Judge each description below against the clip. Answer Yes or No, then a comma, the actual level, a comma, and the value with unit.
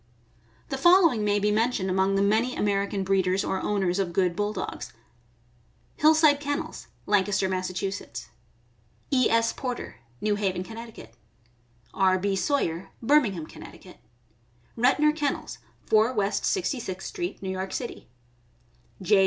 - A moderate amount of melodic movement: Yes, average, 4.8 semitones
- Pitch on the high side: Yes, high, 205 Hz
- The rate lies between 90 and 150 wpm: Yes, slow, 135 wpm